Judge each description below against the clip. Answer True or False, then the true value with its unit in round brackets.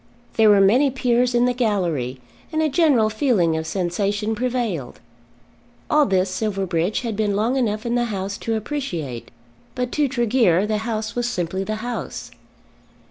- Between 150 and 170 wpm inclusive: True (160 wpm)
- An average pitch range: True (4.2 semitones)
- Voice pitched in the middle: False (215 Hz)